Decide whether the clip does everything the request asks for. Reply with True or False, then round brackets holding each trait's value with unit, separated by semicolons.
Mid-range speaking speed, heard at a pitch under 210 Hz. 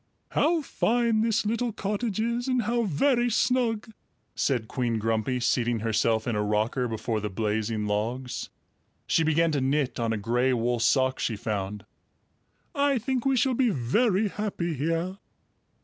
True (155 wpm; 140 Hz)